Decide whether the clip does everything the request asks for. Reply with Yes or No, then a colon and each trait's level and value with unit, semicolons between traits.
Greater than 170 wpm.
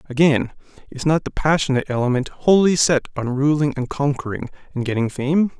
No: average, 160 wpm